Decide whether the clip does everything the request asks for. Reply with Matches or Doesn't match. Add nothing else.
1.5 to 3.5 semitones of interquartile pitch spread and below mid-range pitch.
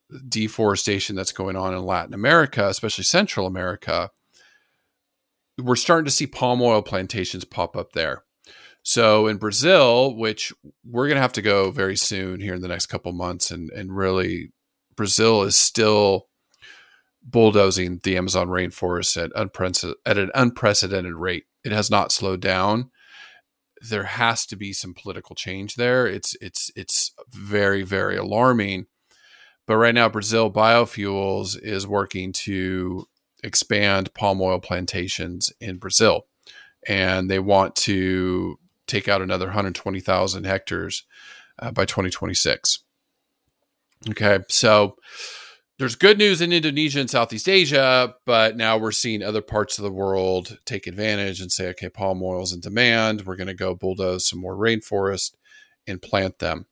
Matches